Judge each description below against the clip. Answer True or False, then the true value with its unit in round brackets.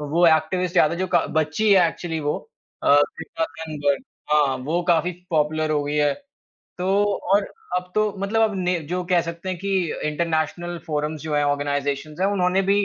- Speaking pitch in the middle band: True (165 Hz)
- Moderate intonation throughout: True (3.3 semitones)